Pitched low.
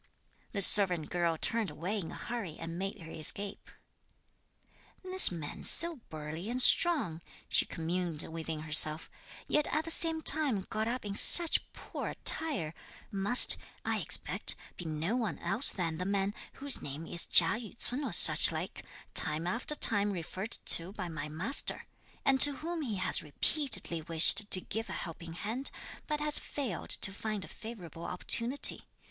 No: high, 200 Hz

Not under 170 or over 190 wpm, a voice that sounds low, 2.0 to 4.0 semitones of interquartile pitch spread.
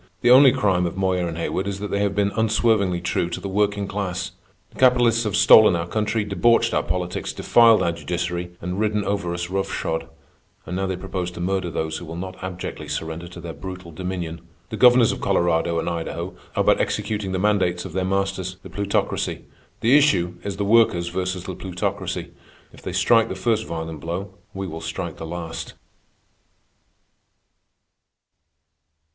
Yes: average, 180 wpm; very low, 95 Hz; average, 2.9 semitones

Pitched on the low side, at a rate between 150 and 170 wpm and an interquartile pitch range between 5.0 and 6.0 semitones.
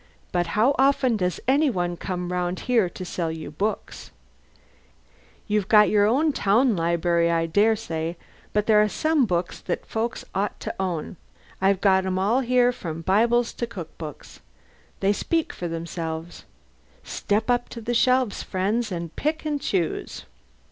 No: high, 200 Hz; average, 160 wpm; average, 5.3 semitones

